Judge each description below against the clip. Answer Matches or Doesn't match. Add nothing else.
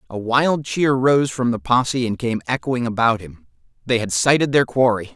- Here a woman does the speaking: Doesn't match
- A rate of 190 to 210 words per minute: Matches